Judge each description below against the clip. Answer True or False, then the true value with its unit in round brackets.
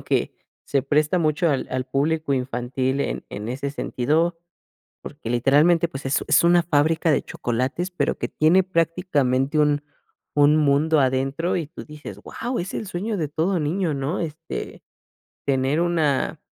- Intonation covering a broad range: False (3.6 semitones)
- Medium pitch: True (150 Hz)